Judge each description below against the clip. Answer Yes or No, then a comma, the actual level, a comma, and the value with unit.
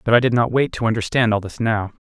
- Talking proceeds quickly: Yes, fast, 290 wpm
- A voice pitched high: No, low, 115 Hz